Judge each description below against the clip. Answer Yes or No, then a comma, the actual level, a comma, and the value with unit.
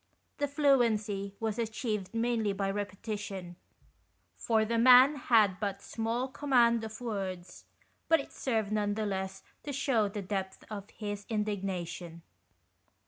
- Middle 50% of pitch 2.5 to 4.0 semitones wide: Yes, average, 3.0 semitones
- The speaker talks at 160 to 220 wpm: No, average, 140 wpm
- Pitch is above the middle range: Yes, high, 215 Hz